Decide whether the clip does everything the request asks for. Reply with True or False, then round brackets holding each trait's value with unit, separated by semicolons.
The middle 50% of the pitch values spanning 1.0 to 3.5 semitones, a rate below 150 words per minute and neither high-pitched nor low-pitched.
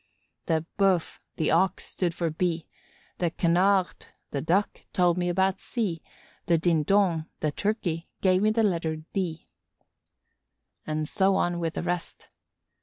True (2.6 semitones; 140 wpm; 175 Hz)